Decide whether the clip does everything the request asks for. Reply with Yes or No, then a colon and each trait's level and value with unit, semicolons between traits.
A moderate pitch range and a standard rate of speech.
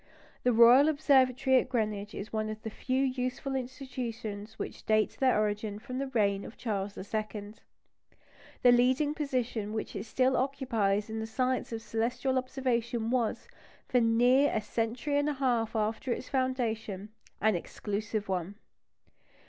Yes: average, 3.1 semitones; average, 150 wpm